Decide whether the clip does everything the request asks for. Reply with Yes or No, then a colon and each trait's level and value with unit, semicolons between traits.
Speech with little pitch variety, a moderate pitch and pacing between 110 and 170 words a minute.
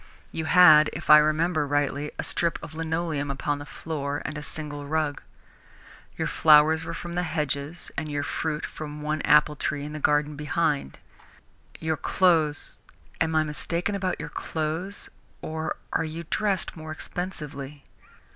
Yes: narrow, 1.8 semitones; medium, 155 Hz; average, 160 wpm